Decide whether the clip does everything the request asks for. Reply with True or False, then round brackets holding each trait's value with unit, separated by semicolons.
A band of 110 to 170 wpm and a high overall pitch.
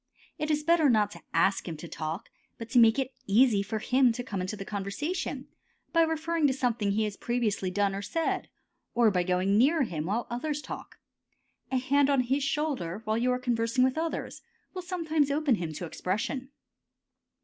False (195 wpm; 240 Hz)